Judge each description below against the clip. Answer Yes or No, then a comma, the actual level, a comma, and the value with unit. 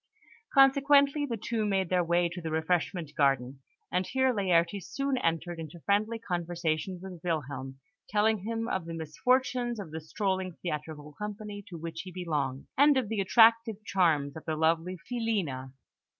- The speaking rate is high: No, average, 160 wpm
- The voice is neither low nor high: Yes, medium, 180 Hz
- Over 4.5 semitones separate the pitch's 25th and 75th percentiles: Yes, wide, 5.6 semitones